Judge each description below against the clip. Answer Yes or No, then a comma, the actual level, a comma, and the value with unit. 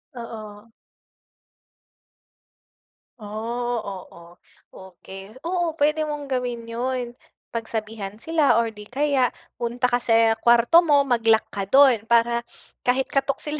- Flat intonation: No, average, 3.6 semitones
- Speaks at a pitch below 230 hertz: No, high, 235 Hz